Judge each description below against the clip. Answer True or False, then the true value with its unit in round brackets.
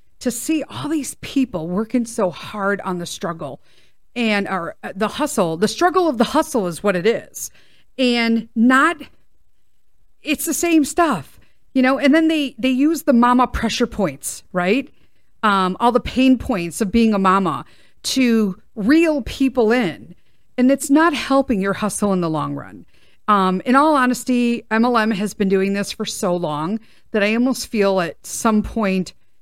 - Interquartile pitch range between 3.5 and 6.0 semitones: True (5.2 semitones)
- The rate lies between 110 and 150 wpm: False (175 wpm)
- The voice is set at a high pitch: True (225 Hz)